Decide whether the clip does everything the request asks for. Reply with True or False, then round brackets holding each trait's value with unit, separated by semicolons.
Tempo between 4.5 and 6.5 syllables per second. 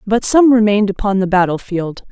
True (5.6 syllables/s)